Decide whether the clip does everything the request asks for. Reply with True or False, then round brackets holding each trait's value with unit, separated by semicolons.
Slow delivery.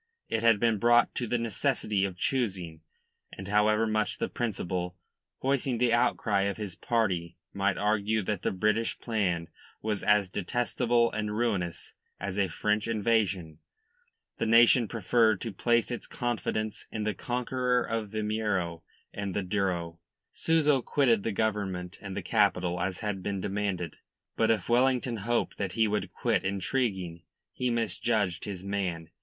False (150 wpm)